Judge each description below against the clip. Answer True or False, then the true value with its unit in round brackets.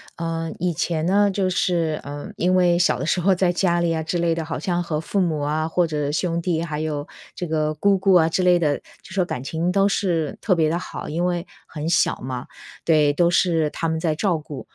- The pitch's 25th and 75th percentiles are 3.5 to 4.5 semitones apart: False (2.5 semitones)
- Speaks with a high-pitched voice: False (165 Hz)